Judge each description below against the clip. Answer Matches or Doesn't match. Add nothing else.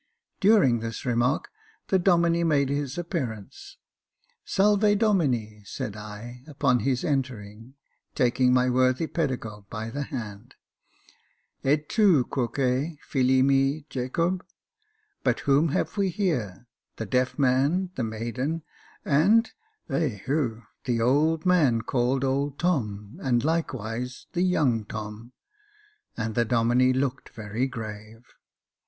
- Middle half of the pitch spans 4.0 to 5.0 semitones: Doesn't match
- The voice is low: Matches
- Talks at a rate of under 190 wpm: Matches